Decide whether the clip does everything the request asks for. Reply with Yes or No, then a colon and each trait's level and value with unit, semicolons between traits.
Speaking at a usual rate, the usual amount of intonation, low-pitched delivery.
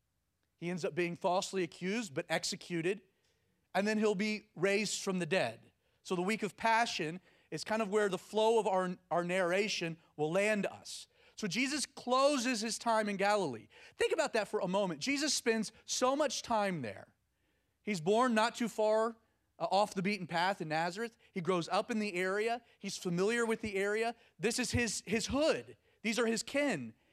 No: average, 185 wpm; average, 3.8 semitones; high, 205 Hz